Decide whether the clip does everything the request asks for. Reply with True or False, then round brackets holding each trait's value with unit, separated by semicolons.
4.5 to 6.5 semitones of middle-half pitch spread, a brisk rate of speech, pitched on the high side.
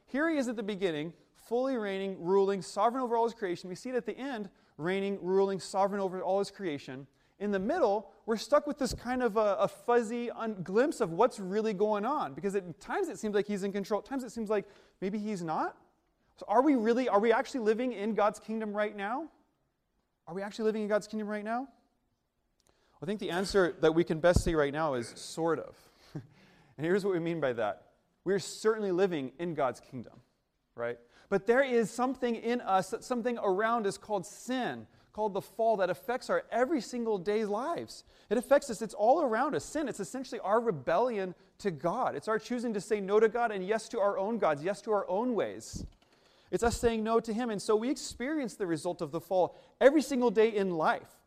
False (3.7 semitones; 220 wpm; 210 Hz)